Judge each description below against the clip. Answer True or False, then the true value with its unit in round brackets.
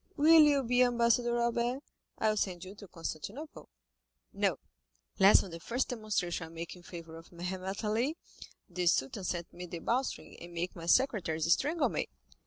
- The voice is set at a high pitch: True (195 Hz)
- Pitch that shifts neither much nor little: False (6.0 semitones)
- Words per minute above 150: True (175 wpm)